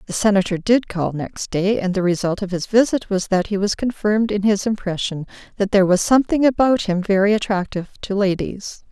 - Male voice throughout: No, female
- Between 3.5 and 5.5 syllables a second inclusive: No, 5.7 syllables/s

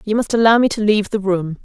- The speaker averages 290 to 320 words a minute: Yes, fast, 295 wpm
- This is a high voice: Yes, high, 210 Hz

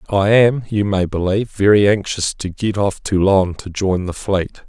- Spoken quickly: No, average, 190 wpm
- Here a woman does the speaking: No, male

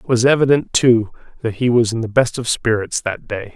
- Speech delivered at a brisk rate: Yes, fast, 235 wpm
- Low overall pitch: Yes, low, 115 Hz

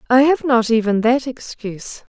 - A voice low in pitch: No, high, 245 Hz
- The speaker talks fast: No, average, 165 wpm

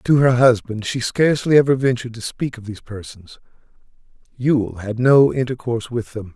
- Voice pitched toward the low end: Yes, low, 120 Hz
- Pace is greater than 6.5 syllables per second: No, 5.4 syllables/s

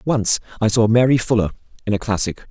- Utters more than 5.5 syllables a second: Yes, 6.0 syllables/s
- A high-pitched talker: No, low, 110 Hz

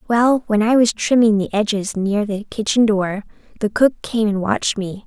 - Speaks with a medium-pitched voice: No, high, 215 Hz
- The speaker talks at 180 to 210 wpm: Yes, average, 200 wpm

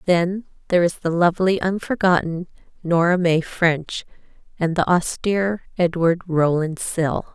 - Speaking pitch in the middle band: Yes, medium, 175 Hz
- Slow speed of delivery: Yes, slow, 125 wpm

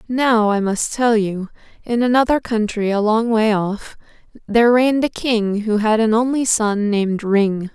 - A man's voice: No, female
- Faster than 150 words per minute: Yes, average, 180 wpm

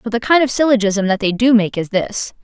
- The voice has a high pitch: Yes, high, 225 Hz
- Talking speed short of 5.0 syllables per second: No, 5.6 syllables/s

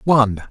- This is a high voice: No, low, 120 Hz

